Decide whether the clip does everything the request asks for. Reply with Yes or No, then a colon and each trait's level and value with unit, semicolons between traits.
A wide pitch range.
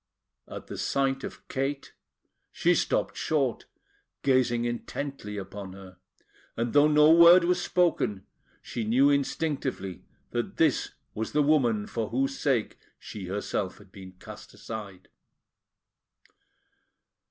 Yes: wide, 5.7 semitones